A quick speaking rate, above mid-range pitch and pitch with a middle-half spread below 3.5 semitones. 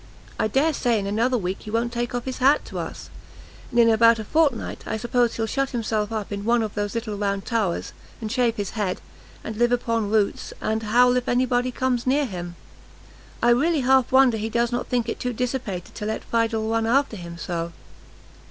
Yes: fast, 215 wpm; high, 230 Hz; narrow, 2.5 semitones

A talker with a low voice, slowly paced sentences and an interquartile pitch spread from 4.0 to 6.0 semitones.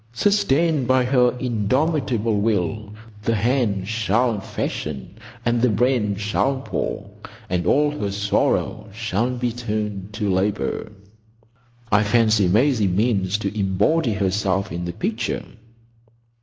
No: low, 110 Hz; slow, 120 wpm; average, 3.6 semitones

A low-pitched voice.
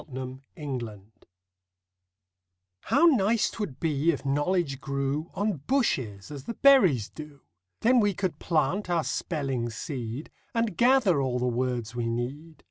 No: medium, 145 Hz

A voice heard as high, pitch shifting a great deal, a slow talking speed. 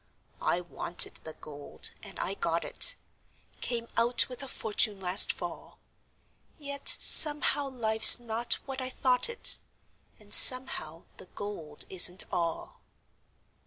Yes: high, 220 Hz; wide, 6.3 semitones; slow, 125 wpm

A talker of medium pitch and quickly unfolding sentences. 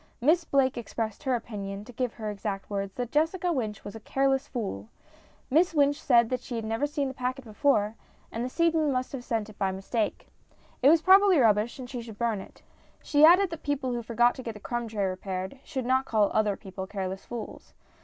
No: high, 240 Hz; fast, 215 wpm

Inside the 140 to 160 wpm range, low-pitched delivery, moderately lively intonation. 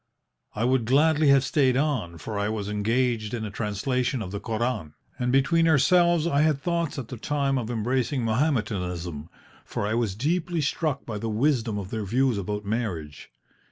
No: average, 180 wpm; low, 120 Hz; average, 5.0 semitones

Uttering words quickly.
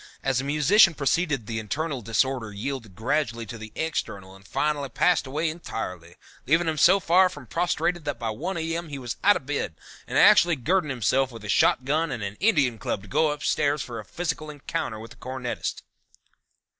No: average, 190 wpm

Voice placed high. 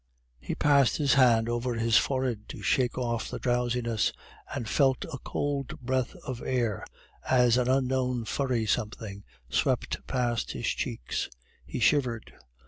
No: low, 125 Hz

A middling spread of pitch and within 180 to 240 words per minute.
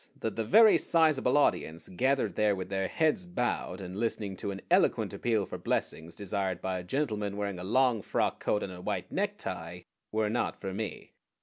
Yes: average, 4.8 semitones; average, 190 wpm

